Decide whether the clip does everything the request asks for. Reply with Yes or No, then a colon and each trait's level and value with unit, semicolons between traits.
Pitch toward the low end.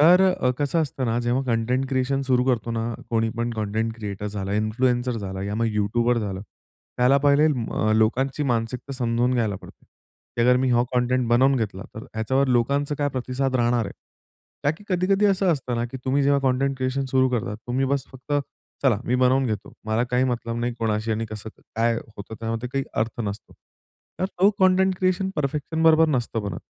Yes: low, 125 Hz